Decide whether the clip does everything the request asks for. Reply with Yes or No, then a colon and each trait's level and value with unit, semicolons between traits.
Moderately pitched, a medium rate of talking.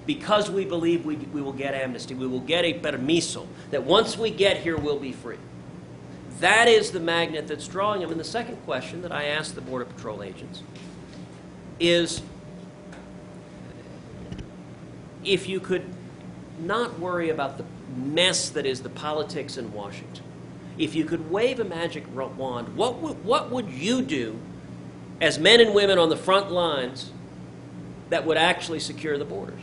Yes: medium, 155 Hz; average, 165 wpm